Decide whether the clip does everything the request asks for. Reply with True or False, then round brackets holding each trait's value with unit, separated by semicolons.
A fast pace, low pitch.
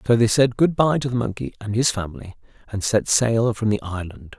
True (235 wpm; 110 Hz)